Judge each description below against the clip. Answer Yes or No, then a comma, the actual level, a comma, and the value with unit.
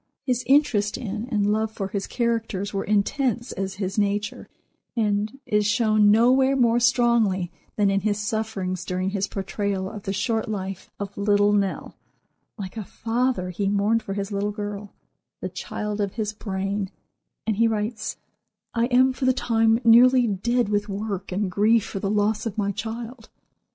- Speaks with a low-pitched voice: No, high, 210 Hz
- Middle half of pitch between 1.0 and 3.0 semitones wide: Yes, narrow, 2.4 semitones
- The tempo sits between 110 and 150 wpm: No, average, 165 wpm